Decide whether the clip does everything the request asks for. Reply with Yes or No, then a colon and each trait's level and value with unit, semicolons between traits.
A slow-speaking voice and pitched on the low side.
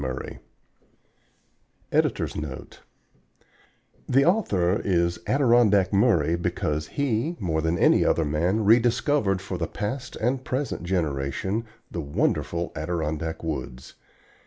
Yes: slow, 100 wpm; very low, 90 Hz